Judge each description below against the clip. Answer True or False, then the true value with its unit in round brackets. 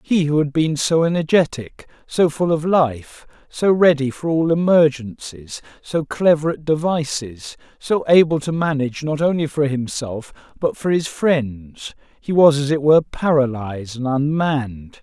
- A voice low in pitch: False (145 Hz)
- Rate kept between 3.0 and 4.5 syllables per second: True (4.4 syllables/s)